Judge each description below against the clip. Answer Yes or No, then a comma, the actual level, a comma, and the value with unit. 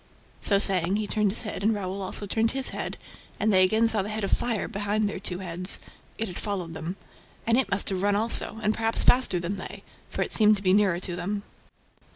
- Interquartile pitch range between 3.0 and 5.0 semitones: No, narrow, 2.5 semitones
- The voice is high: Yes, high, 205 Hz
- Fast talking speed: Yes, fast, 230 wpm